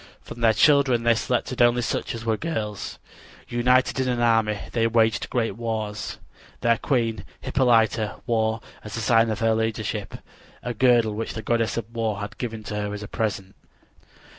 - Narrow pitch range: Yes, narrow, 1.7 semitones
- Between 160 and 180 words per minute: Yes, average, 170 wpm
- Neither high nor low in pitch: No, low, 115 Hz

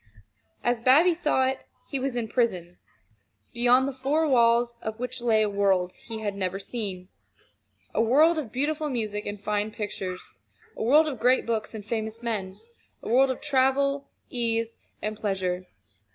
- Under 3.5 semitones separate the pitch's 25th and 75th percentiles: No, average, 4.0 semitones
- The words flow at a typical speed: Yes, average, 165 wpm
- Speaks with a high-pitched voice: Yes, high, 230 Hz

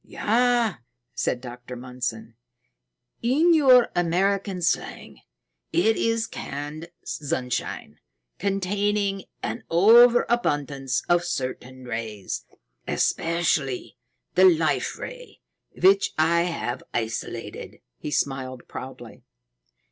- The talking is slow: Yes, slow, 85 wpm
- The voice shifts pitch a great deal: Yes, wide, 7.9 semitones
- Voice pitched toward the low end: No, medium, 170 Hz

